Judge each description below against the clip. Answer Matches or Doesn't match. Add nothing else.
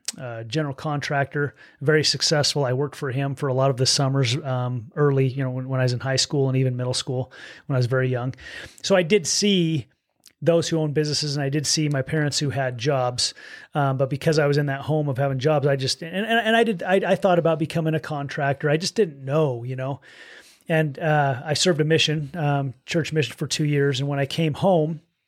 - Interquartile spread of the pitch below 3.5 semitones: Matches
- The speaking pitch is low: Doesn't match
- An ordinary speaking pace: Doesn't match